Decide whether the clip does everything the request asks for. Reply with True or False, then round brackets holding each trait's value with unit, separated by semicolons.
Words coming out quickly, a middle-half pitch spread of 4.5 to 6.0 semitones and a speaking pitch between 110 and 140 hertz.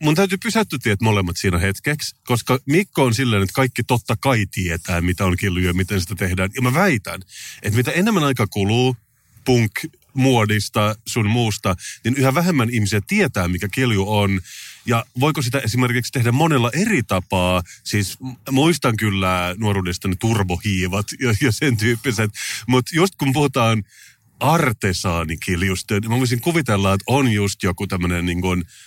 True (160 wpm; 5.2 semitones; 115 Hz)